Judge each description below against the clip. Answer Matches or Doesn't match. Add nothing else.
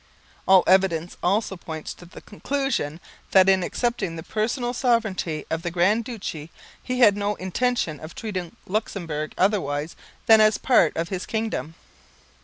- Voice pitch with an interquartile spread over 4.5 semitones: Matches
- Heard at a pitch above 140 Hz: Matches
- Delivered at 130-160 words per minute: Matches